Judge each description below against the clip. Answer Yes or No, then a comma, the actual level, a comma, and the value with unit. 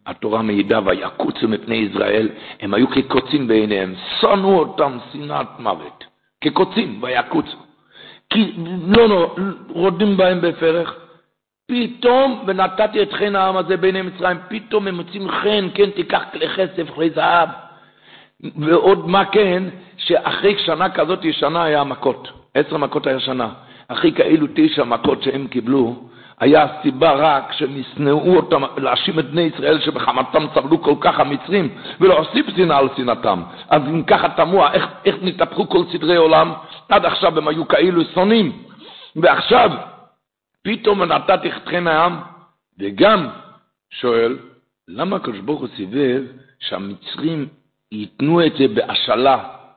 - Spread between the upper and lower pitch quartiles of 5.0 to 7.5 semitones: Yes, wide, 5.5 semitones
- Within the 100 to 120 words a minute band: No, average, 130 wpm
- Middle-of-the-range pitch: Yes, medium, 170 Hz